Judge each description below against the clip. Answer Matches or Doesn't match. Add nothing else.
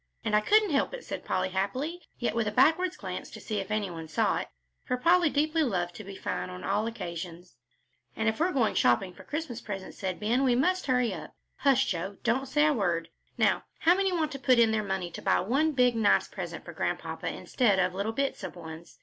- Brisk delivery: Matches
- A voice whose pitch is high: Matches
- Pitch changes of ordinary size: Doesn't match